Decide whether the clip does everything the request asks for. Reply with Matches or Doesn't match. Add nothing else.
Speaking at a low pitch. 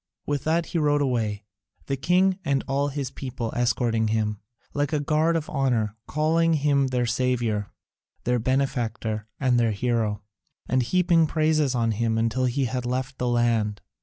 Matches